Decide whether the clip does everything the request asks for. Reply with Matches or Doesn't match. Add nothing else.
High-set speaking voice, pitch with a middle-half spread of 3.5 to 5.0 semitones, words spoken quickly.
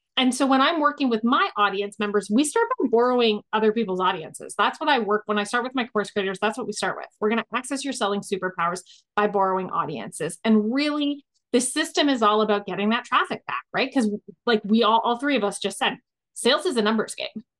Matches